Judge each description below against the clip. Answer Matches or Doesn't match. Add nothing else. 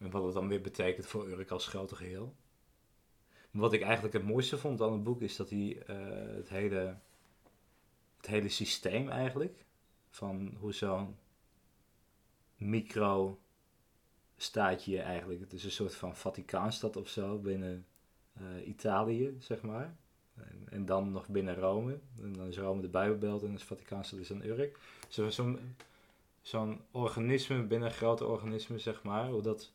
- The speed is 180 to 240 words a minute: Doesn't match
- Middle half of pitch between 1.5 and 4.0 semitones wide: Matches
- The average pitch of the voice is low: Matches